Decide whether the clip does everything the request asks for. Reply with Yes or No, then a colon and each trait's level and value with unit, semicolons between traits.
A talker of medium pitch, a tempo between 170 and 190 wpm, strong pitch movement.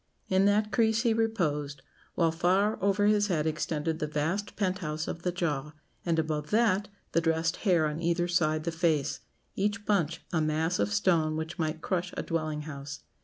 No: medium, 170 Hz; average, 185 wpm; average, 4.0 semitones